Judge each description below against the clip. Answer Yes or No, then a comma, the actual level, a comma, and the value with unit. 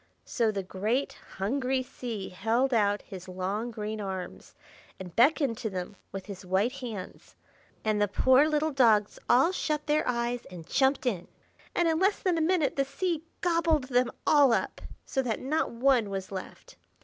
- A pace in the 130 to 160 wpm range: No, average, 175 wpm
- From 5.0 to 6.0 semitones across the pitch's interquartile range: Yes, wide, 5.6 semitones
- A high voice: Yes, high, 240 Hz